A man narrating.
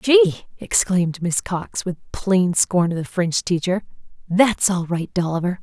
No: female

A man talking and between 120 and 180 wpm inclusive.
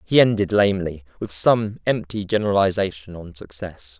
Yes: male; slow, 135 wpm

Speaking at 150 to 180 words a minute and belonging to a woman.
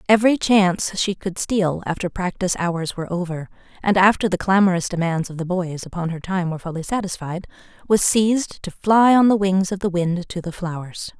No: average, 200 wpm; female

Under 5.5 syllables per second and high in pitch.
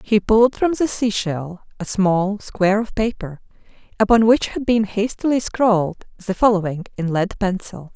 Yes: 4.7 syllables/s; high, 205 Hz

